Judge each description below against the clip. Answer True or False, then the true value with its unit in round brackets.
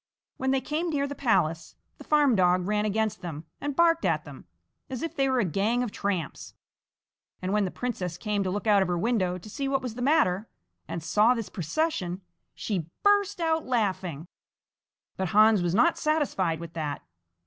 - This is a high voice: True (210 Hz)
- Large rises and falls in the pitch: True (6.9 semitones)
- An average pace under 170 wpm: False (190 wpm)